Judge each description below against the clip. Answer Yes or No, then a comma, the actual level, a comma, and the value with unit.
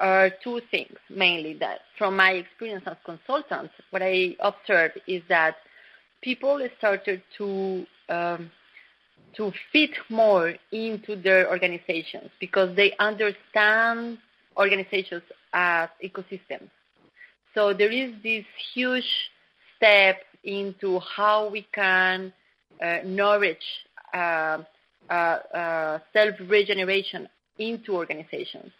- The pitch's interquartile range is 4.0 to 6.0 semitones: No, average, 2.7 semitones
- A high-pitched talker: Yes, high, 195 Hz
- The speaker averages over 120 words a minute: No, average, 105 wpm